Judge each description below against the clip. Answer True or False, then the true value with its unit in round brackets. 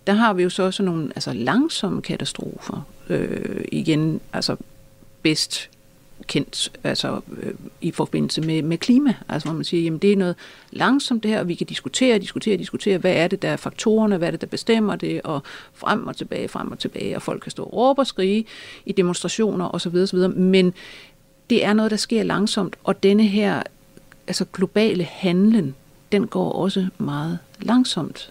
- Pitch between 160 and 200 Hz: True (190 Hz)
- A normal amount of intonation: True (3.7 semitones)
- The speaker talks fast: False (185 wpm)